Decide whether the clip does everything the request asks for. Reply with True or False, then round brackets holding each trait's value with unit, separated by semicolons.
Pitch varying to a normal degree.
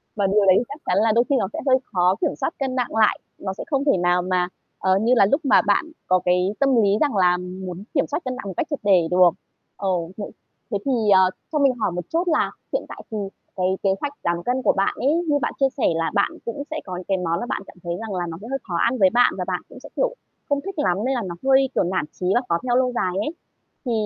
False (6.6 semitones)